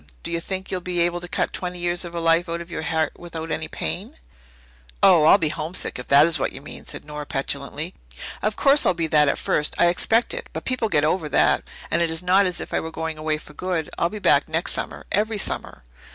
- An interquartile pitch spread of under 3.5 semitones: Yes, narrow, 2.6 semitones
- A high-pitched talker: No, medium, 170 Hz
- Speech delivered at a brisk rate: Yes, fast, 250 wpm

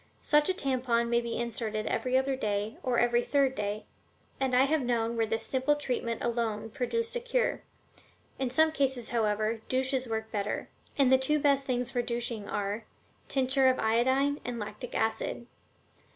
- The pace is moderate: Yes, average, 170 wpm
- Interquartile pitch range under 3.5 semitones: Yes, average, 3.0 semitones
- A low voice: No, high, 245 Hz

